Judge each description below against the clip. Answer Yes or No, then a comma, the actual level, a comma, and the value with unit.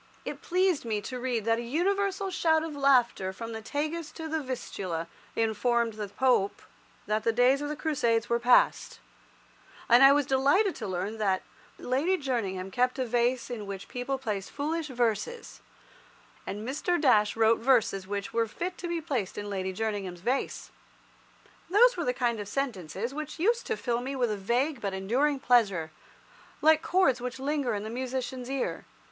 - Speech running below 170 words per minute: No, average, 175 wpm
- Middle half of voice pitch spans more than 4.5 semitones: Yes, average, 5.2 semitones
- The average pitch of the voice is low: No, high, 245 Hz